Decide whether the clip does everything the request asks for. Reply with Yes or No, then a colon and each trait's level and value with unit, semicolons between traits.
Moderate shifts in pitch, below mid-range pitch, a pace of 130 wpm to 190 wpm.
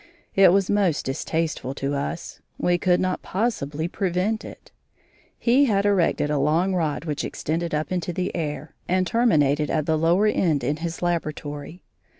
No: average, 3.6 semitones; medium, 170 Hz; average, 160 wpm